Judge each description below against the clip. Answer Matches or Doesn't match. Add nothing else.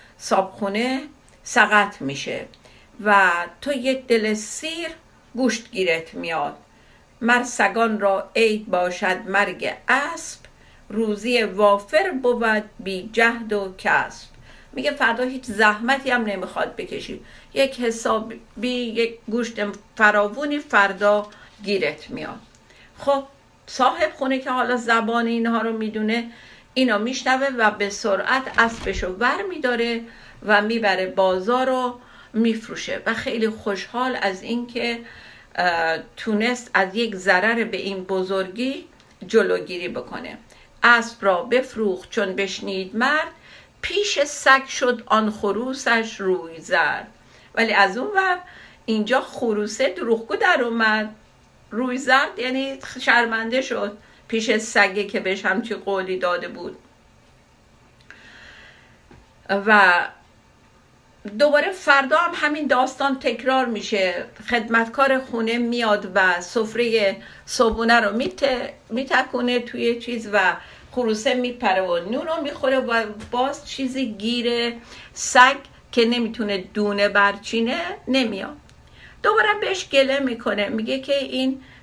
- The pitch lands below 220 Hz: Doesn't match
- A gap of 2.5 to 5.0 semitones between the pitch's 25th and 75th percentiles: Matches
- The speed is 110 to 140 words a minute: Matches